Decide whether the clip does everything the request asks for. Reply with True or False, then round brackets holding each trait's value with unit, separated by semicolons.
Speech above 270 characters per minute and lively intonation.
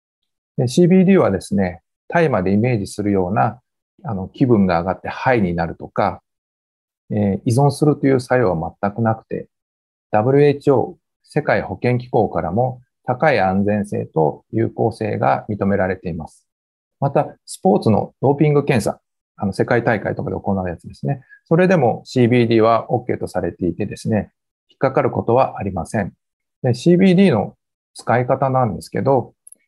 True (315 characters per minute; 6.2 semitones)